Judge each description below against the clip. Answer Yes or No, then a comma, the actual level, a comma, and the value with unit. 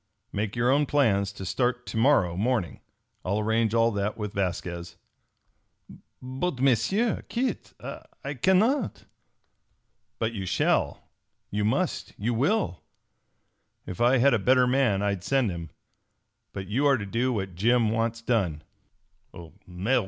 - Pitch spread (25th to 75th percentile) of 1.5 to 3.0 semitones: No, average, 4.6 semitones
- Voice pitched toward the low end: Yes, low, 115 Hz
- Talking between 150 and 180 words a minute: No, slow, 135 wpm